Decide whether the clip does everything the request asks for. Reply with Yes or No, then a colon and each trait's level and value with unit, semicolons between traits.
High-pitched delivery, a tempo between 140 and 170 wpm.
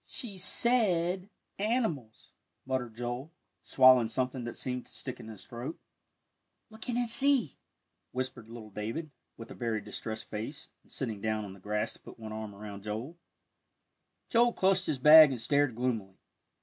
No: low, 125 Hz; average, 160 wpm